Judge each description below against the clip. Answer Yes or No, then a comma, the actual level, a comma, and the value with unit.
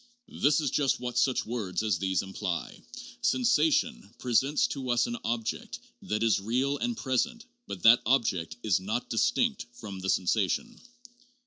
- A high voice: No, low, 120 Hz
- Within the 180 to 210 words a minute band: No, average, 150 wpm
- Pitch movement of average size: No, wide, 5.8 semitones